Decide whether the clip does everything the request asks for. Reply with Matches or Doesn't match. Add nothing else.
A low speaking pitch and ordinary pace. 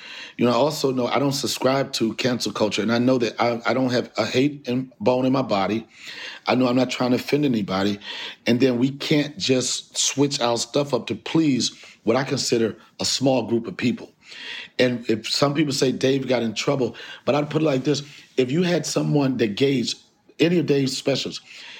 Doesn't match